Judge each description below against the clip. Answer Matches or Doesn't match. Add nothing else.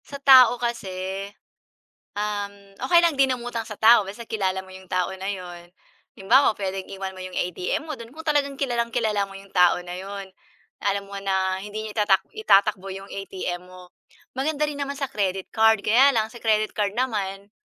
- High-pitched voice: Matches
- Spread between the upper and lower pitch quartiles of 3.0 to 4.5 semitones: Matches